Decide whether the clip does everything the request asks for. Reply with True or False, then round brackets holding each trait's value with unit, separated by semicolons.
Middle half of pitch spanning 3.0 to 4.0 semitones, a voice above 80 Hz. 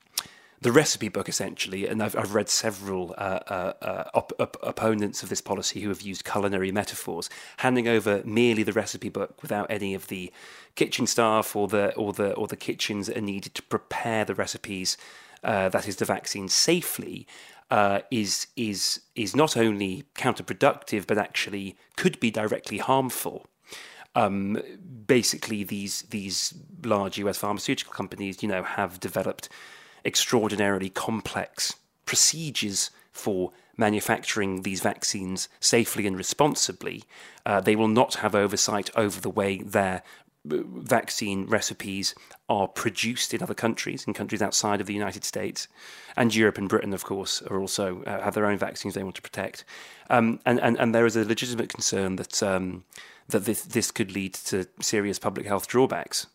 False (2.6 semitones; 105 Hz)